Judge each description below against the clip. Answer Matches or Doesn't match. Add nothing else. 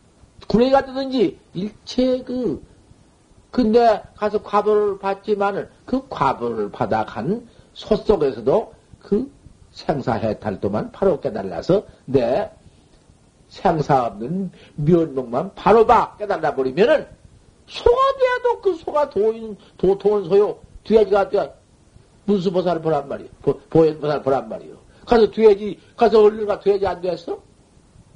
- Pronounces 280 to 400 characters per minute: Doesn't match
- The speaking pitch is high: Matches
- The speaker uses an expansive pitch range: Doesn't match